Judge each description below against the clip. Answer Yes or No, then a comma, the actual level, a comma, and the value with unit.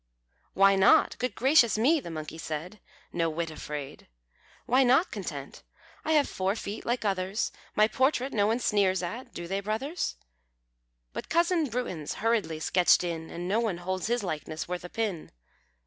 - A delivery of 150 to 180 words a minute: Yes, average, 165 wpm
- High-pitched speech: Yes, high, 200 Hz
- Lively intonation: Yes, wide, 5.7 semitones